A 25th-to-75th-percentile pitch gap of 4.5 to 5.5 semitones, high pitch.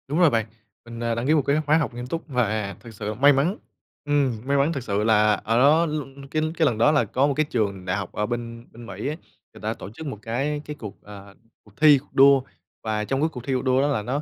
No: average, 5.1 semitones; low, 125 Hz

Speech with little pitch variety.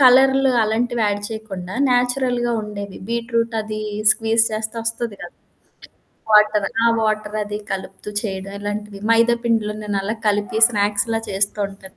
Yes: narrow, 2.2 semitones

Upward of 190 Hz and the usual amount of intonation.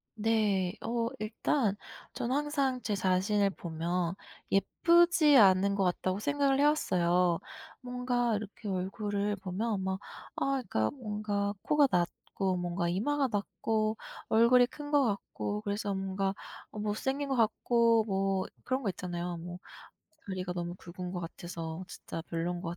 Yes: high, 205 Hz; average, 4.5 semitones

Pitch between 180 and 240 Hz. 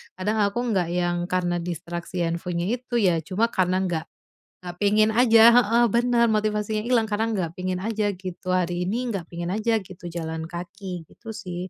Yes: medium, 185 Hz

